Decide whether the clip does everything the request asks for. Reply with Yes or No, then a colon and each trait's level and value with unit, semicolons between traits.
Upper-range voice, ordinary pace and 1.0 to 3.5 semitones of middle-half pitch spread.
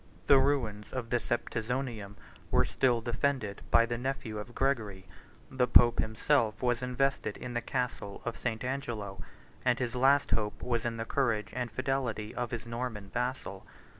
No: low, 120 Hz; average, 165 wpm; average, 2.7 semitones